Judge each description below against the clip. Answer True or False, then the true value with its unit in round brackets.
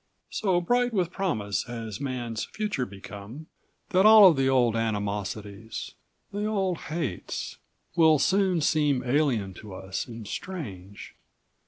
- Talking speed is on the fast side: False (135 wpm)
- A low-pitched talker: True (130 Hz)